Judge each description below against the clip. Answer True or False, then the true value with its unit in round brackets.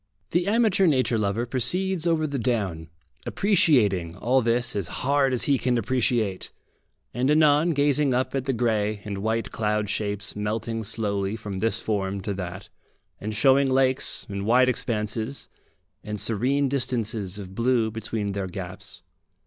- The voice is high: False (115 Hz)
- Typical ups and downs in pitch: True (4.4 semitones)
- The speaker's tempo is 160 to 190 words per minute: False (150 wpm)